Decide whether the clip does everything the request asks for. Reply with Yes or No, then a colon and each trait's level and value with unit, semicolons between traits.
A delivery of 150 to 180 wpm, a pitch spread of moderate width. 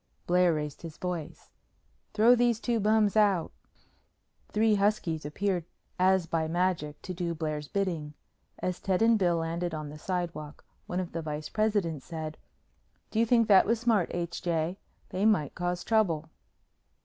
Yes: average, 160 wpm; average, 4.4 semitones